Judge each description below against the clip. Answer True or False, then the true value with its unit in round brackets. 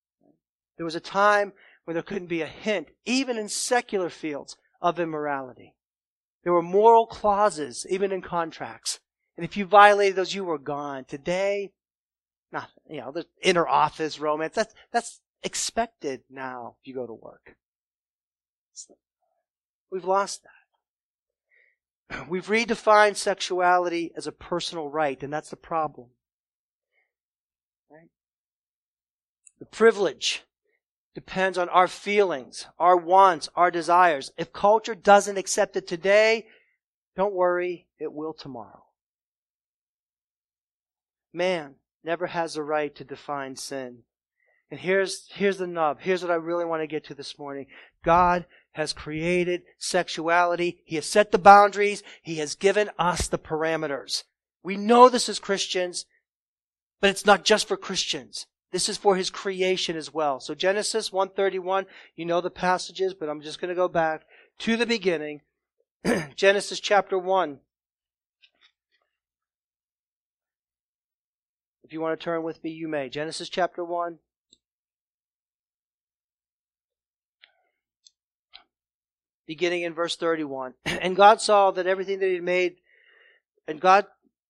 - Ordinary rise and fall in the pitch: False (6.8 semitones)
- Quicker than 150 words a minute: False (135 wpm)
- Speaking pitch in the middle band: True (170 Hz)